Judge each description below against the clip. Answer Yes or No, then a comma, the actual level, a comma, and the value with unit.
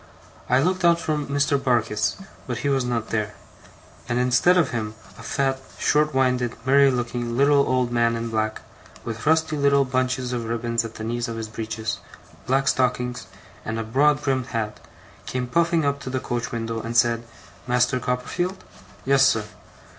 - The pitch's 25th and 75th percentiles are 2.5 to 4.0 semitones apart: Yes, average, 3.2 semitones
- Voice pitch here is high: No, low, 125 Hz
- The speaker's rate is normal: Yes, average, 175 wpm